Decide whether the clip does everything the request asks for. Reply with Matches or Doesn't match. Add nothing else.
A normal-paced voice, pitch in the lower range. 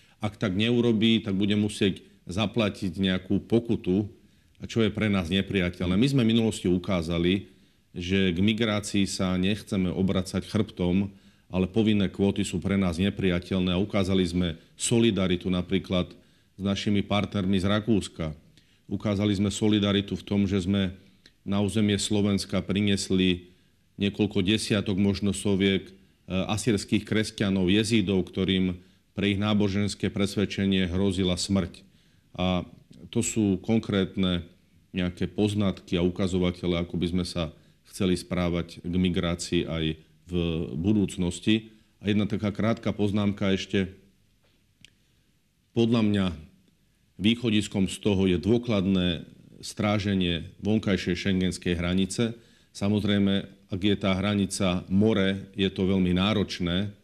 Matches